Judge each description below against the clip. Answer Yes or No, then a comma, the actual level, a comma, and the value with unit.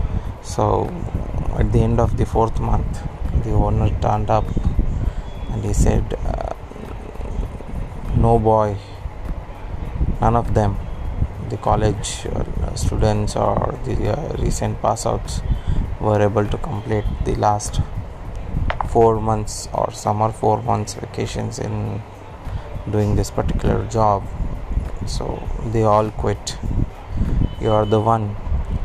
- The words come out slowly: Yes, slow, 115 wpm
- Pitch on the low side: Yes, low, 105 Hz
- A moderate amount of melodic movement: No, narrow, 2.3 semitones